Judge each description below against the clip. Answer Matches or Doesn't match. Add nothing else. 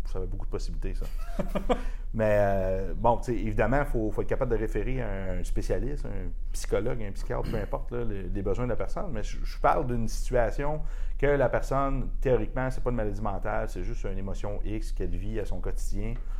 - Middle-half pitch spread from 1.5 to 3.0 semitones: Doesn't match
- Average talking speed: Matches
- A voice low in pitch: Matches